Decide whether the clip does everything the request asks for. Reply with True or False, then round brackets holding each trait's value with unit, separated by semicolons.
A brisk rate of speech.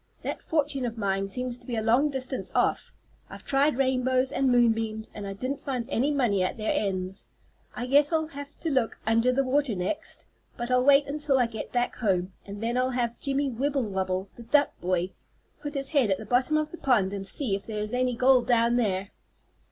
True (215 wpm)